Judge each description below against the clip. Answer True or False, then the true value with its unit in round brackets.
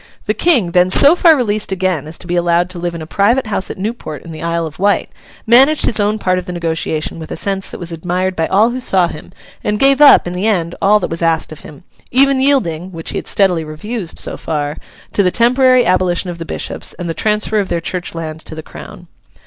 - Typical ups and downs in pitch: True (4.4 semitones)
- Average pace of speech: False (245 wpm)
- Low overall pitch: False (185 Hz)